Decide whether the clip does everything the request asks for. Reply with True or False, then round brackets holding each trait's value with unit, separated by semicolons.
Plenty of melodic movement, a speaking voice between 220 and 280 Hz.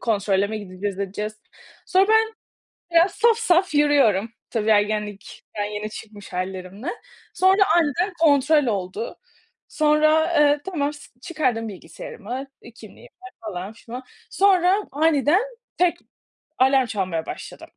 True (7.7 semitones; 255 Hz)